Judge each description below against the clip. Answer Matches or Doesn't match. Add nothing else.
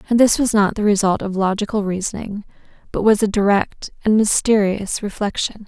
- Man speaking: Doesn't match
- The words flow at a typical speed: Matches